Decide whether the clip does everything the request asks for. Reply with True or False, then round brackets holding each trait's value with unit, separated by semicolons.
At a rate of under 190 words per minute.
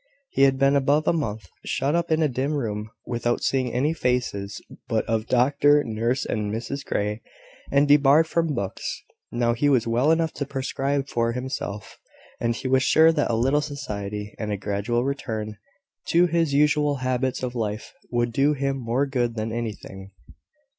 True (175 wpm)